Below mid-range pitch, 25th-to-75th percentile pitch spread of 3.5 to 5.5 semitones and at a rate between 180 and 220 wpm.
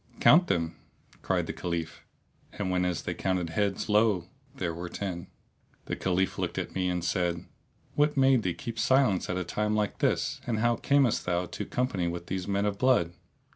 Yes: very low, 95 Hz; average, 4.1 semitones; average, 185 wpm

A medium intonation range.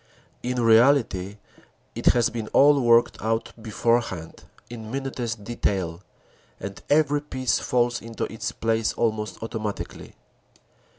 No: narrow, 2.2 semitones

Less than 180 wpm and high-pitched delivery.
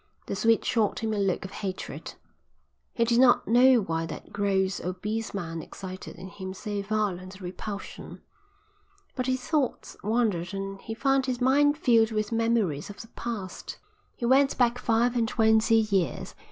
Yes: average, 165 wpm; high, 220 Hz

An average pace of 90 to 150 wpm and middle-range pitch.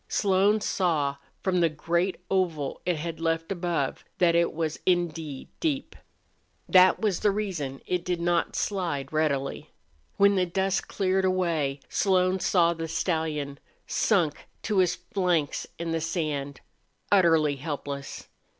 Yes: average, 140 wpm; medium, 170 Hz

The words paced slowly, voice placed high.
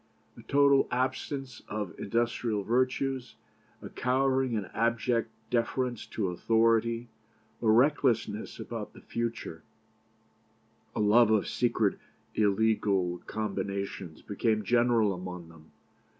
No: slow, 105 wpm; low, 115 Hz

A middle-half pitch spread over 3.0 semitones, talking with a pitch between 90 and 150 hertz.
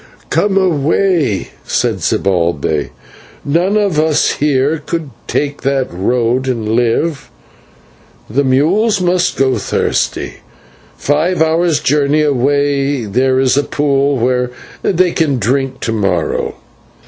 Yes: average, 4.2 semitones; medium, 140 Hz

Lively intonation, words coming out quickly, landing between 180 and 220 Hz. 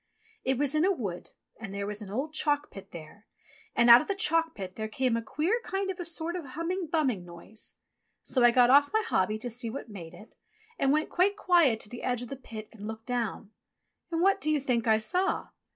No: wide, 7.0 semitones; fast, 240 wpm; very high, 255 Hz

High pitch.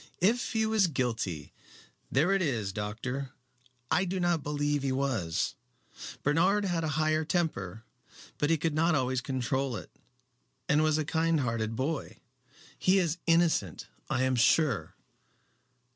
No: medium, 145 Hz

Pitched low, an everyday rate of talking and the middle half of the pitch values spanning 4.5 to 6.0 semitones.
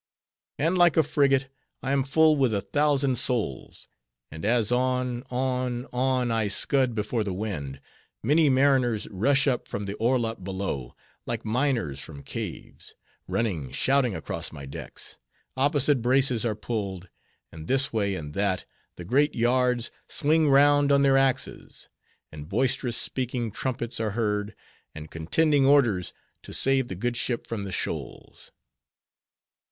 Yes: low, 120 Hz; average, 145 wpm; average, 4.9 semitones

